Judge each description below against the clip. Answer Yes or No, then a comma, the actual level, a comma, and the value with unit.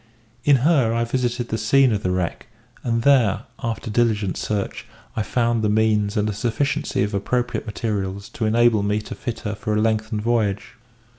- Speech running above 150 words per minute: Yes, average, 180 wpm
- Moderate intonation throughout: No, narrow, 2.3 semitones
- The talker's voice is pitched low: Yes, low, 110 Hz